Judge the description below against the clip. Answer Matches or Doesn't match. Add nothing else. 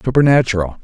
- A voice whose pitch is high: Doesn't match